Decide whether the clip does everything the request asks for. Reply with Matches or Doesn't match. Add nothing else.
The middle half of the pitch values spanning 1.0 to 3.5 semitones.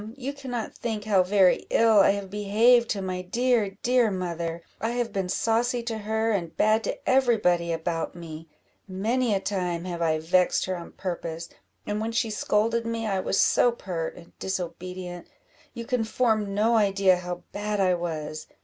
Doesn't match